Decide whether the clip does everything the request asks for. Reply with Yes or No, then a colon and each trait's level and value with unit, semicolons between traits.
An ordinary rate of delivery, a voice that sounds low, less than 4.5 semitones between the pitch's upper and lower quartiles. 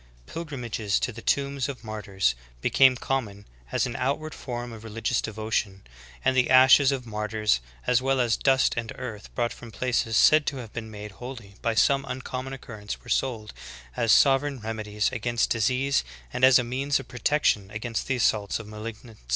Yes: average, 180 wpm; low, 120 Hz; average, 3.4 semitones